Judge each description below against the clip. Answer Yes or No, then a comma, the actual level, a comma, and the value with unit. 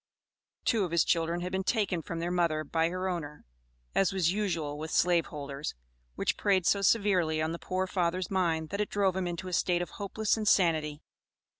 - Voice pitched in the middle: Yes, medium, 175 Hz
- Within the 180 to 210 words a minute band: Yes, average, 195 wpm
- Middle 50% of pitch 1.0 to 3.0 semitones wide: Yes, average, 2.7 semitones